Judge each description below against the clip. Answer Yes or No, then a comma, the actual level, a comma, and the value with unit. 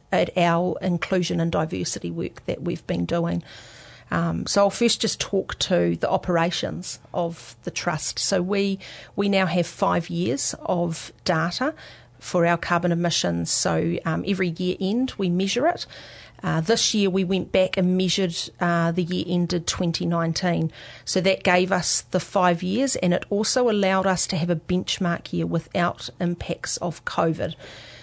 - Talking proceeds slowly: No, average, 165 wpm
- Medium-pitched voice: Yes, medium, 175 Hz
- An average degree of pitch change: No, narrow, 2.3 semitones